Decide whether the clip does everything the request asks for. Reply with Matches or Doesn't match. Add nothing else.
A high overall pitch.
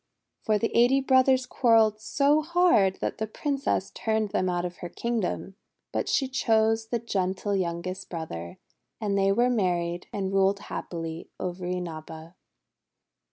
Matches